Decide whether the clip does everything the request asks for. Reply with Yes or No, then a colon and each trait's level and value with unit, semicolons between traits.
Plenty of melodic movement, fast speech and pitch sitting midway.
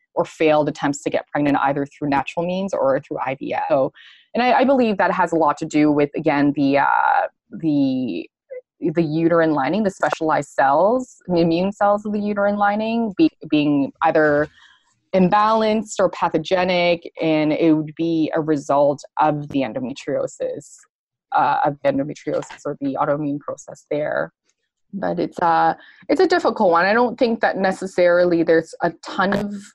No: wide, 6.8 semitones; average, 165 wpm; medium, 175 Hz